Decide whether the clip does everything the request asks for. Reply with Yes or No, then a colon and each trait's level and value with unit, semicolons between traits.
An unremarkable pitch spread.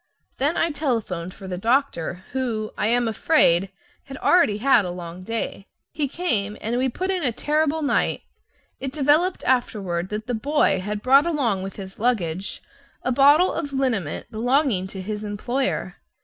No: wide, 6.1 semitones